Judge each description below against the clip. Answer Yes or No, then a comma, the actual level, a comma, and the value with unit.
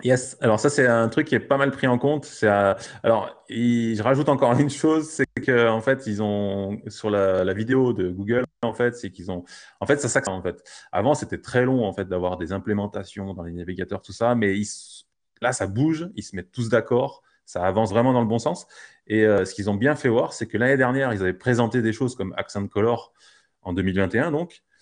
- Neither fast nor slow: No, fast, 235 wpm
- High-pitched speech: No, low, 115 Hz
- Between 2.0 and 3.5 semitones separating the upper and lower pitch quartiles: No, average, 4.6 semitones